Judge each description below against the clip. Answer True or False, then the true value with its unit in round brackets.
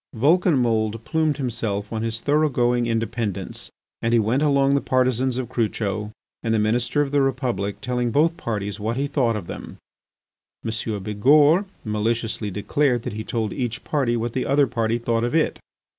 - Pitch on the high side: False (120 Hz)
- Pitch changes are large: False (3.6 semitones)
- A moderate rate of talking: True (170 wpm)